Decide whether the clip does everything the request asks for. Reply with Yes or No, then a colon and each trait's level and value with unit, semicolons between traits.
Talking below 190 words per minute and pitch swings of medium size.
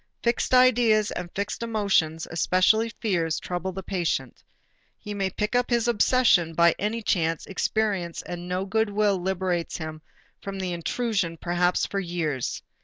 Yes: average, 150 wpm; average, 3.9 semitones